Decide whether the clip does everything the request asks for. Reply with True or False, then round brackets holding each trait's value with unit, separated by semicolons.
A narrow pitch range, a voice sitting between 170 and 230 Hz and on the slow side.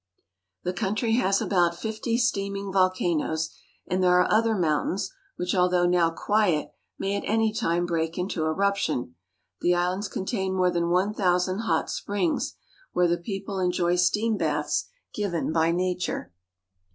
False (2.3 semitones; 185 Hz; 150 wpm)